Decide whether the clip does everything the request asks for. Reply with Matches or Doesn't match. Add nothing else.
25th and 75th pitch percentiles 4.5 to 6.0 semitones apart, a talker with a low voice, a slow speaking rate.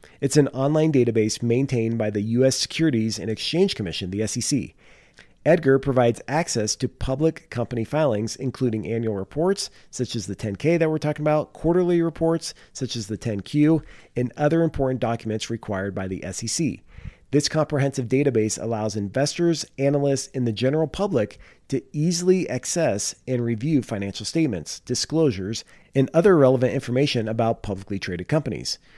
Doesn't match